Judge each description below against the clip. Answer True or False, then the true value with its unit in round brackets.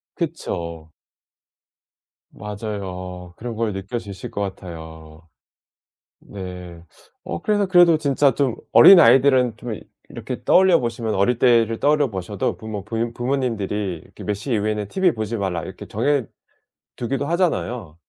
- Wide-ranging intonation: True (5.7 semitones)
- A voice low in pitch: True (110 Hz)